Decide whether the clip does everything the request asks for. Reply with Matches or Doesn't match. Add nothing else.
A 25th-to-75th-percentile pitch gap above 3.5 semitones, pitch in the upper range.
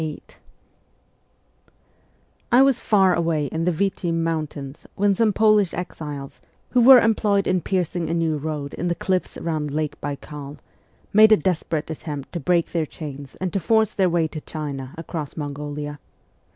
Doesn't match